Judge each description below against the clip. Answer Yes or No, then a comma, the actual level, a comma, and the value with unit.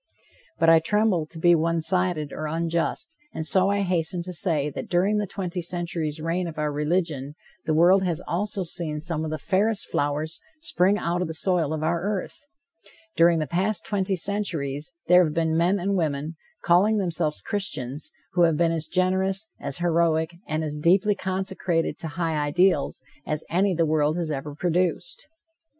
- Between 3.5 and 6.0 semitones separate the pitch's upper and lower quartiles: No, average, 2.9 semitones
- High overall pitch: No, medium, 170 Hz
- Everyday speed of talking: Yes, average, 180 wpm